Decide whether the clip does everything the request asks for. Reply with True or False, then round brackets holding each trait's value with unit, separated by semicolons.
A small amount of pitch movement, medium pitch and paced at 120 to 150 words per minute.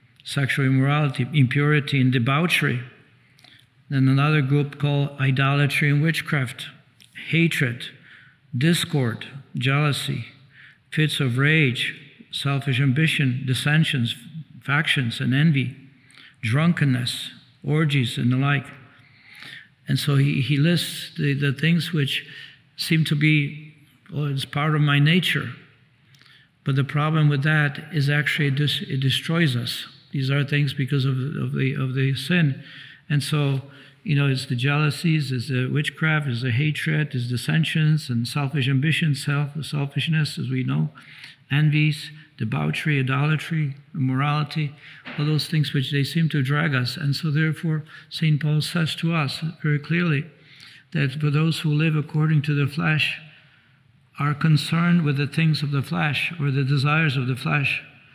True (2.2 semitones; 145 Hz; 140 wpm)